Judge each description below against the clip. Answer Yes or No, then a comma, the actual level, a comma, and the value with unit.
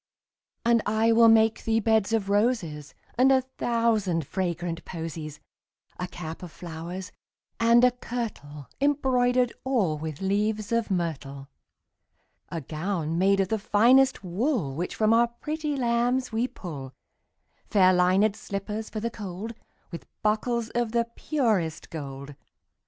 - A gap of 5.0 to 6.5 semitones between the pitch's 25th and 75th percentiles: Yes, wide, 5.5 semitones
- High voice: Yes, high, 210 Hz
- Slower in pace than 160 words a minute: Yes, average, 140 wpm